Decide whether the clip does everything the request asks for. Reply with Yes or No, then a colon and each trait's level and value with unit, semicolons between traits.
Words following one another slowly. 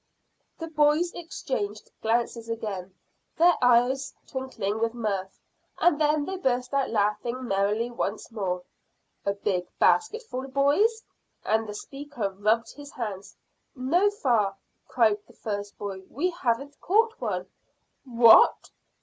Yes: slow, 125 wpm